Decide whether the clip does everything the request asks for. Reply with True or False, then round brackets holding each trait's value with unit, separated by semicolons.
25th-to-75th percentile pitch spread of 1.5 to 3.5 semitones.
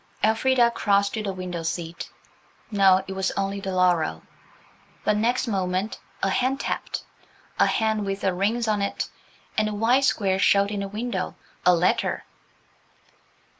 True (2.7 semitones)